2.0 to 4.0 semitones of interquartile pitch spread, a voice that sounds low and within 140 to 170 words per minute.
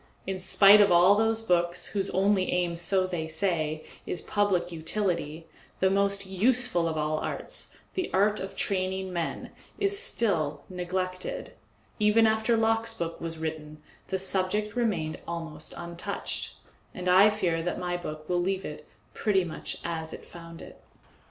No: average, 3.4 semitones; medium, 185 Hz; average, 155 wpm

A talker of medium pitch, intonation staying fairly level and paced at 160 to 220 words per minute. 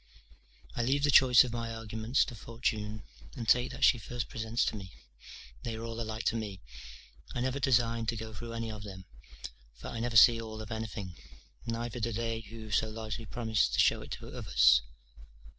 No: low, 115 Hz; narrow, 1.3 semitones; average, 195 wpm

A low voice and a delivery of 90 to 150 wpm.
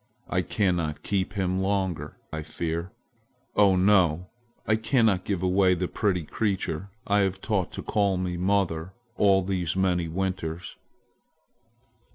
Yes: very low, 95 Hz; slow, 135 wpm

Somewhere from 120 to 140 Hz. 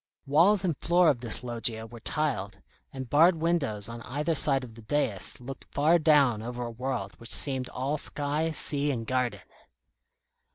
Yes: low, 135 Hz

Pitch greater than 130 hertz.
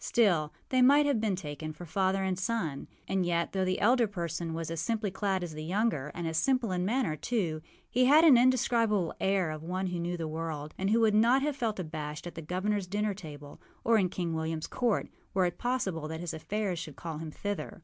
Yes: medium, 185 Hz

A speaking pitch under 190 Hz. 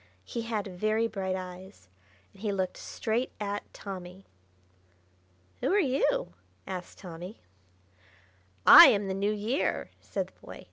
No: high, 200 Hz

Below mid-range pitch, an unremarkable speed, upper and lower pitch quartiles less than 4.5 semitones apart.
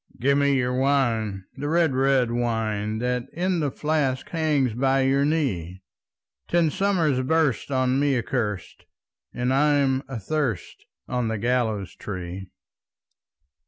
No: low, 130 Hz; slow, 125 wpm; average, 4.0 semitones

